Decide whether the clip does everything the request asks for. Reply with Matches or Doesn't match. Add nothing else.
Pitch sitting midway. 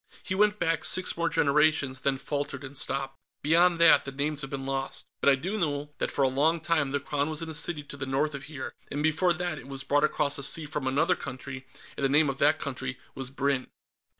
Matches